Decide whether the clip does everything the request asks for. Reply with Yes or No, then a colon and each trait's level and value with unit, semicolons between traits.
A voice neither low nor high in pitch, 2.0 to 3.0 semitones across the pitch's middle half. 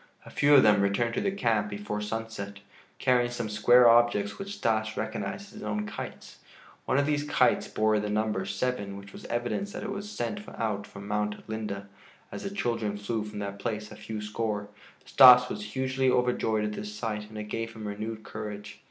No: low, 110 Hz; average, 2.7 semitones